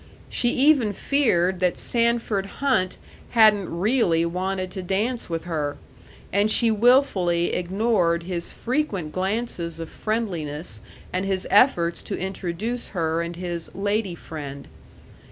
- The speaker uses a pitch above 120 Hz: Yes, high, 190 Hz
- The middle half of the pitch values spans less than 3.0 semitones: No, average, 4.7 semitones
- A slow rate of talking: Yes, slow, 125 wpm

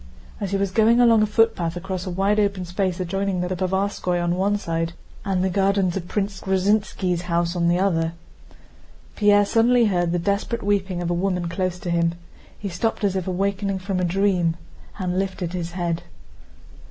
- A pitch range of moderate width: No, narrow, 2.2 semitones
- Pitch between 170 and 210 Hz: Yes, medium, 185 Hz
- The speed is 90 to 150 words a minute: No, average, 185 wpm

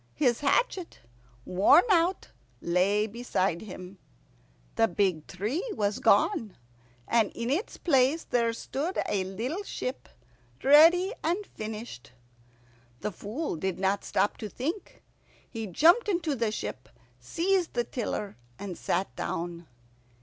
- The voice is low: No, high, 230 Hz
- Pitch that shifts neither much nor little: No, wide, 8.6 semitones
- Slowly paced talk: Yes, slow, 125 wpm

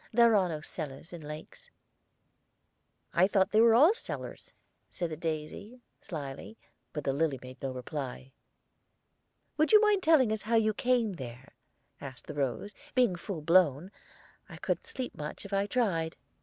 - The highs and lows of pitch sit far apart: Yes, wide, 7.3 semitones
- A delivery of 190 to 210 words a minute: No, average, 160 wpm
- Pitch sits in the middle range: Yes, medium, 180 Hz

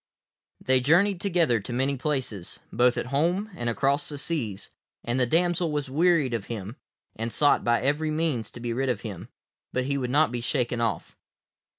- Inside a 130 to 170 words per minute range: No, average, 190 wpm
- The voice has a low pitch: Yes, low, 130 Hz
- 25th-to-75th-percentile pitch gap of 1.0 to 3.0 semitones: No, average, 4.5 semitones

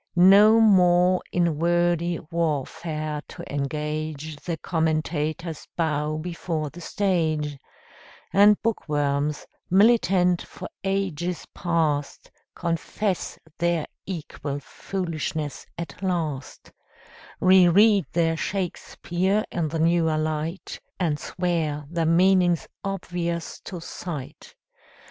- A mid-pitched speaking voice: Yes, medium, 170 Hz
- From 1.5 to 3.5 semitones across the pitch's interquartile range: Yes, average, 2.7 semitones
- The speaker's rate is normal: No, slow, 95 wpm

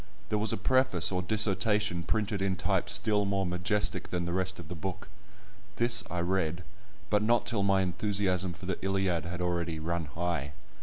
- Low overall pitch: Yes, very low, 95 Hz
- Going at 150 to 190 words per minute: Yes, average, 185 wpm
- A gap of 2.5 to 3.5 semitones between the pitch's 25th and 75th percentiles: Yes, average, 3.0 semitones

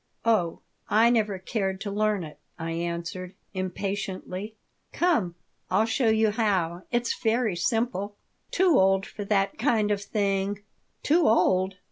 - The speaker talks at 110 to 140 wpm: Yes, slow, 135 wpm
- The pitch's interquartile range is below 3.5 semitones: Yes, average, 3.0 semitones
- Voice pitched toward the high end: Yes, high, 200 Hz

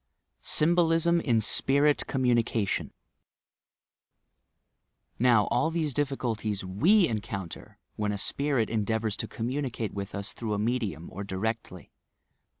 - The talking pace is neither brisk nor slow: No, slow, 110 wpm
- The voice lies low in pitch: Yes, low, 115 Hz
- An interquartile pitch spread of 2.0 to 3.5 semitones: No, wide, 5.4 semitones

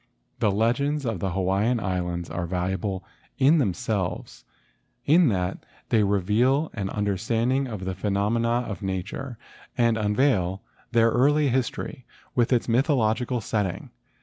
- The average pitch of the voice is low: Yes, low, 110 Hz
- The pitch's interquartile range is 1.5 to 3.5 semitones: No, average, 4.5 semitones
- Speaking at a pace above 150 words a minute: No, slow, 135 wpm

